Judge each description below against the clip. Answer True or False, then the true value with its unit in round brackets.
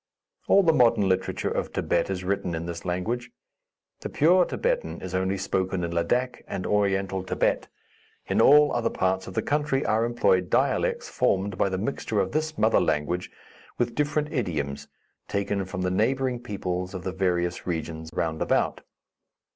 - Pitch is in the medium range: False (95 Hz)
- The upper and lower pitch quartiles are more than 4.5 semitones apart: True (5.1 semitones)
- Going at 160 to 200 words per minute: True (165 wpm)